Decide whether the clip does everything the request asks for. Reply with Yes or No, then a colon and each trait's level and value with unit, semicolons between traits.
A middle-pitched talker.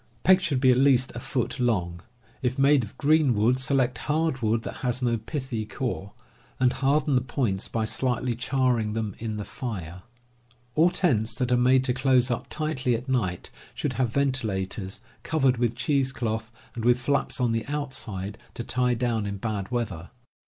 No: low, 125 Hz